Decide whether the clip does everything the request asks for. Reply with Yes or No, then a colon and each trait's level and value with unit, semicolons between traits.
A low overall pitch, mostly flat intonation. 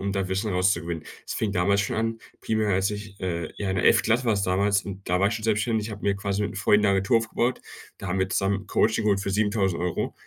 Yes: low, 100 Hz; narrow, 2.0 semitones